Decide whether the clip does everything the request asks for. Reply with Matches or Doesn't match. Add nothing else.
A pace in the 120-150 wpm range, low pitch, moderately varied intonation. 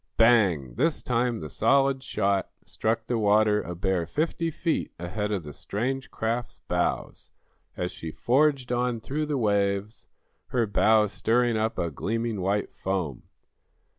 Matches